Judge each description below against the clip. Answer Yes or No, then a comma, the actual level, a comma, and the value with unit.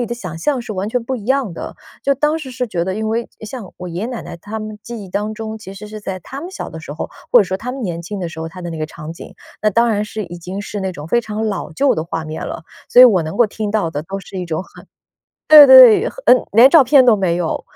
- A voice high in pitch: Yes, high, 210 Hz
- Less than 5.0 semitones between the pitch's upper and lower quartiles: No, average, 5.3 semitones